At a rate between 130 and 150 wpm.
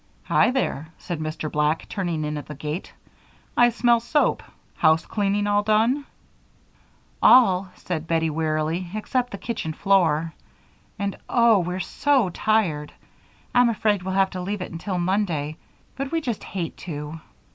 Yes: average, 145 wpm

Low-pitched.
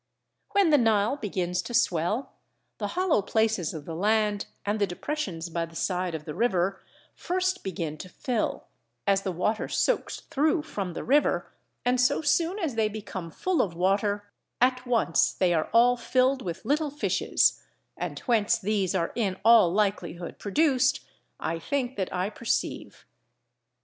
No: high, 210 Hz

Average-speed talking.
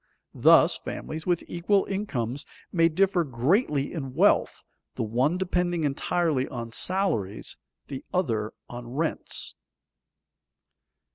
No: slow, 110 wpm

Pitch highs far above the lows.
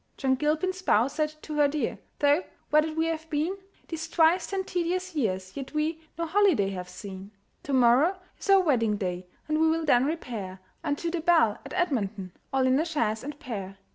Yes: wide, 6.3 semitones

